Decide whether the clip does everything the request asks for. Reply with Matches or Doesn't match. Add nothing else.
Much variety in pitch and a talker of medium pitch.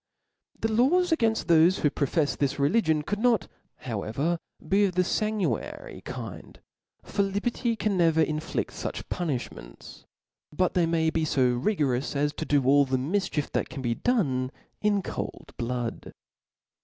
Matches